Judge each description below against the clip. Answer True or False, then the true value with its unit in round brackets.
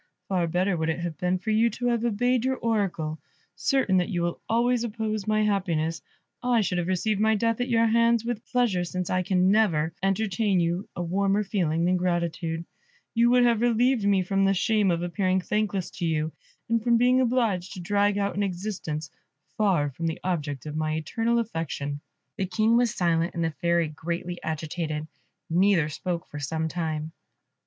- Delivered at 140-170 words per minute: False (190 wpm)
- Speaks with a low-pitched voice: False (185 Hz)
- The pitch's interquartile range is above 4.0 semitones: True (4.7 semitones)